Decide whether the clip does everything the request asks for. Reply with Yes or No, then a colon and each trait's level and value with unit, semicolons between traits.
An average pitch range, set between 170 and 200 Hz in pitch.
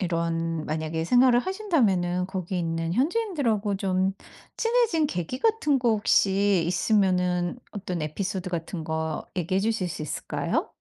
No: wide, 6.0 semitones; high, 190 Hz